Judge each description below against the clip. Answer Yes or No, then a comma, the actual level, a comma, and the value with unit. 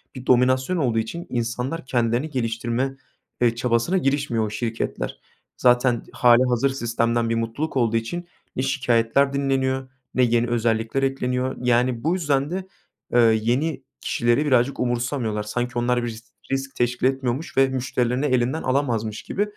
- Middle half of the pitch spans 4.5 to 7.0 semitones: No, narrow, 2.4 semitones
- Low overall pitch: Yes, low, 125 Hz